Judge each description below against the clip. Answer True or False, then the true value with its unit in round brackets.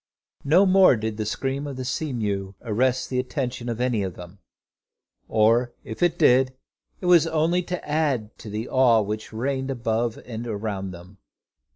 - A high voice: False (120 Hz)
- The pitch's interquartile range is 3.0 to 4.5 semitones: True (4.2 semitones)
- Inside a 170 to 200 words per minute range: True (175 wpm)